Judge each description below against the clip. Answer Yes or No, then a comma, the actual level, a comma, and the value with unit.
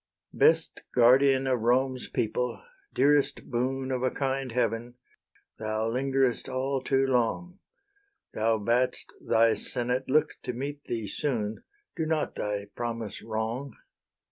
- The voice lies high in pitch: No, low, 125 Hz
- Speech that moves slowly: Yes, slow, 125 wpm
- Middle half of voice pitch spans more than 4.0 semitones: No, average, 2.8 semitones